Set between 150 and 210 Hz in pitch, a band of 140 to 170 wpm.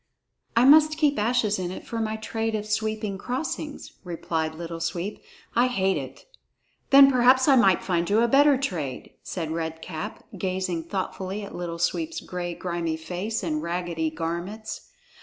Yes: high, 190 Hz; average, 160 wpm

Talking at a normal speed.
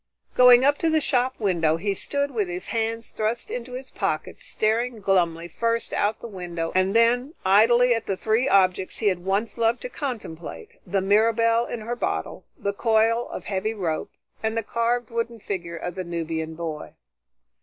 Yes: average, 180 wpm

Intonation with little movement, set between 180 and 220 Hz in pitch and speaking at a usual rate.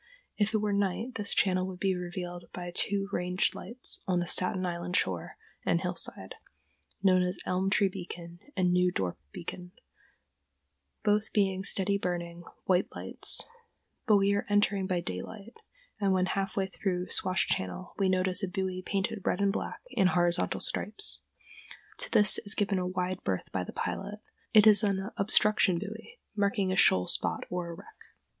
Yes: narrow, 2.2 semitones; high, 190 Hz; average, 170 wpm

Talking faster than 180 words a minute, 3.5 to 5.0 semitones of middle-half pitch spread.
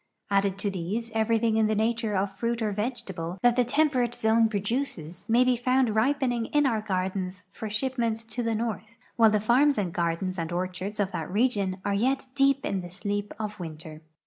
Yes: average, 195 wpm; average, 3.8 semitones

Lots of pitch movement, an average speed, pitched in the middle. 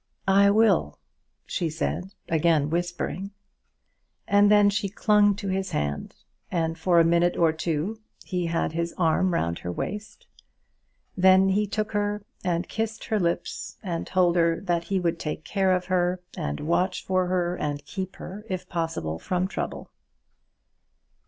No: average, 2.8 semitones; average, 155 wpm; medium, 180 Hz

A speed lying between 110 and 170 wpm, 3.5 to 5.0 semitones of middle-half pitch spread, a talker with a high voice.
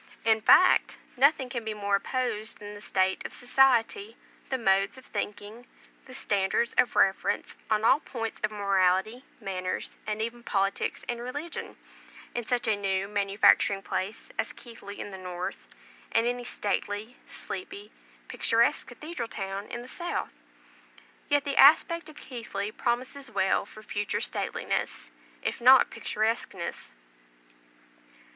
Yes: average, 140 wpm; average, 3.8 semitones; high, 220 Hz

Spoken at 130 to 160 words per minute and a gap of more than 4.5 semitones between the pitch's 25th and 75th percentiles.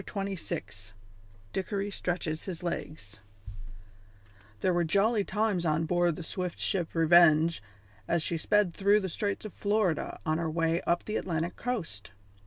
No: average, 150 wpm; average, 3.6 semitones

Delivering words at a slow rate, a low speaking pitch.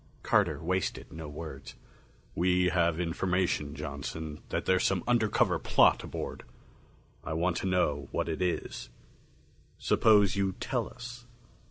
Yes: slow, 130 wpm; very low, 90 Hz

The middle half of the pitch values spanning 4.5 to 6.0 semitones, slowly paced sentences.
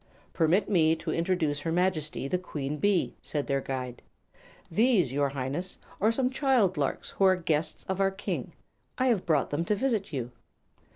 No: average, 5.1 semitones; average, 180 wpm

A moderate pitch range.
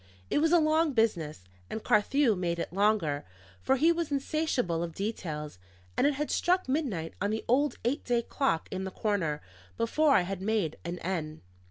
No: wide, 8.7 semitones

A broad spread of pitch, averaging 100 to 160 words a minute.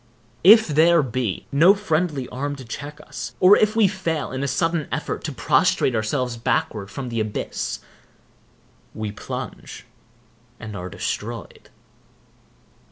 Yes: wide, 6.7 semitones; slow, 135 wpm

